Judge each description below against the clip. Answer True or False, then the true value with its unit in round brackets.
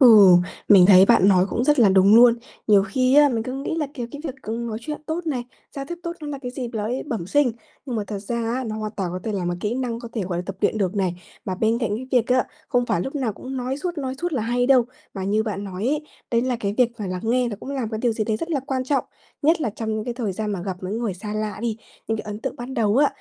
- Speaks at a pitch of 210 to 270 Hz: True (230 Hz)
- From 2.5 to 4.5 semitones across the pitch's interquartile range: True (4.0 semitones)